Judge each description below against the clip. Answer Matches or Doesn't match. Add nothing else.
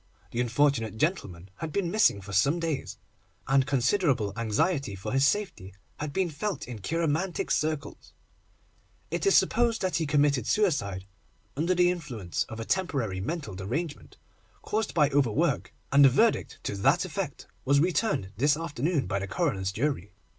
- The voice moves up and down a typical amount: Doesn't match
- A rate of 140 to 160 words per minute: Matches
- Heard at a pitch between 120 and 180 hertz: Matches